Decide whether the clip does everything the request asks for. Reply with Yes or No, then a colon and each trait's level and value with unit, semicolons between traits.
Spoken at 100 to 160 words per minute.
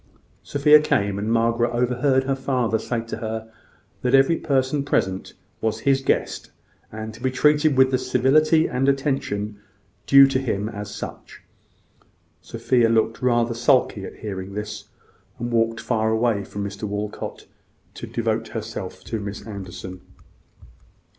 Yes: average, 145 wpm